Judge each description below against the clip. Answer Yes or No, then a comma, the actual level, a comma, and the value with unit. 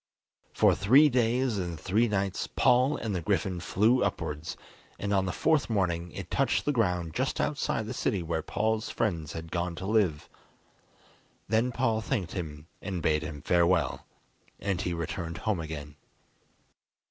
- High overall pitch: No, very low, 95 Hz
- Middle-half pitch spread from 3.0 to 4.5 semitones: No, average, 5.1 semitones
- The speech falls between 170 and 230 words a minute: No, average, 160 wpm